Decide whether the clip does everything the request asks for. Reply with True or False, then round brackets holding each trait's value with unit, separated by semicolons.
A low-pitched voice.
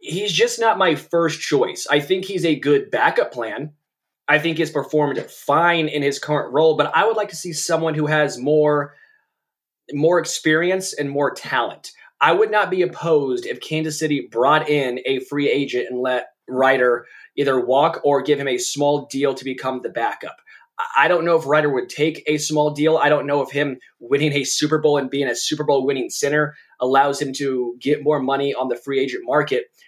False (150 Hz)